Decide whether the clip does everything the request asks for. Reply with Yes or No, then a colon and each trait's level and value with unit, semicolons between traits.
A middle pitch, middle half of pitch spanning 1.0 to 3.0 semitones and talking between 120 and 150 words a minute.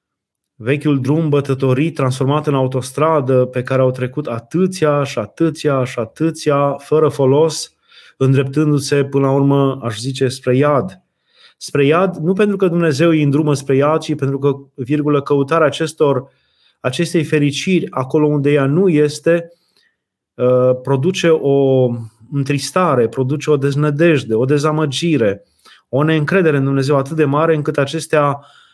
Yes: medium, 145 Hz; narrow, 2.6 semitones; average, 135 wpm